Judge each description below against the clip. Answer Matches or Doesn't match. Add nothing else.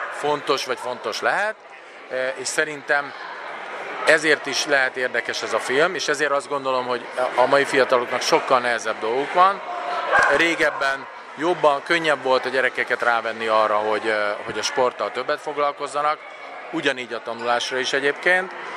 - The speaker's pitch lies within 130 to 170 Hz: Matches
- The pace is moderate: Matches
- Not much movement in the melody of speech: Doesn't match